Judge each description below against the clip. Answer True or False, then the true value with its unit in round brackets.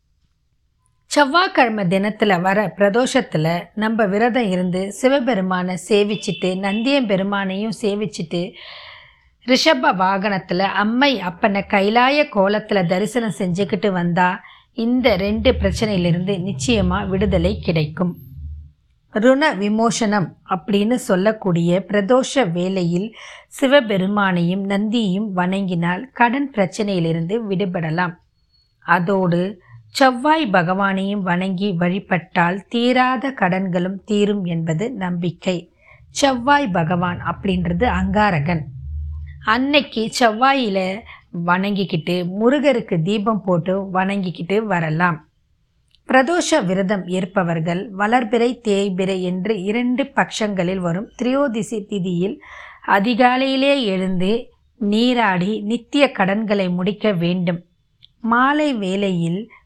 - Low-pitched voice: False (200 Hz)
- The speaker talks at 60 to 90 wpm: True (80 wpm)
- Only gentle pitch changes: False (4.2 semitones)